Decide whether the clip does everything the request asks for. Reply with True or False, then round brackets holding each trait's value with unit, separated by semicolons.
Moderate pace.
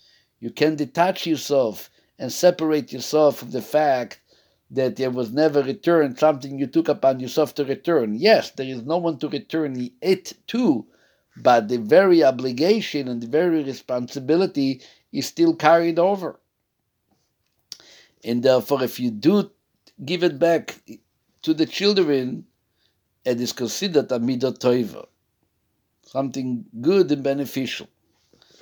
False (130 wpm)